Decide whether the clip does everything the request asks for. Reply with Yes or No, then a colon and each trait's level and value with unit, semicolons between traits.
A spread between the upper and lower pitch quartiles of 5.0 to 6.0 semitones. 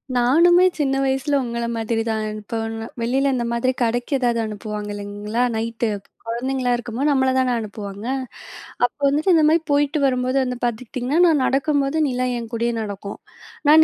No: average, 3.2 semitones